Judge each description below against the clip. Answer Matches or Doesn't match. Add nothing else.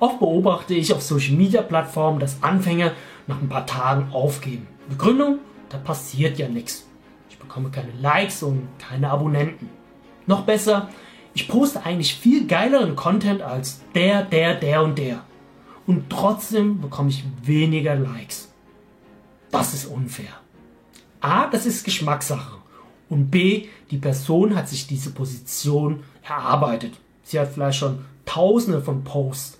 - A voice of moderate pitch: Matches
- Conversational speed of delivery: Matches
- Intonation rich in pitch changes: Matches